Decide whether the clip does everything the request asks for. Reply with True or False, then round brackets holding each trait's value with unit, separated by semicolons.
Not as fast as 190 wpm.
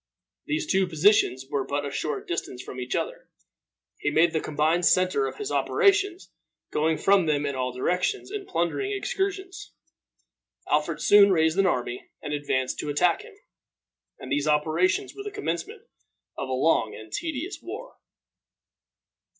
True (160 wpm)